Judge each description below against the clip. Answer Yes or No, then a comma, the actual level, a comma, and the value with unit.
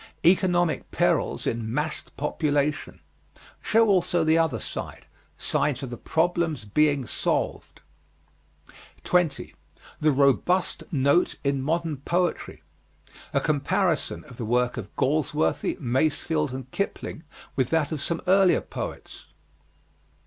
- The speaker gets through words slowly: Yes, slow, 115 wpm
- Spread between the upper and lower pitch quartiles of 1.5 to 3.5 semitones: No, average, 4.3 semitones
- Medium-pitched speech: Yes, medium, 150 Hz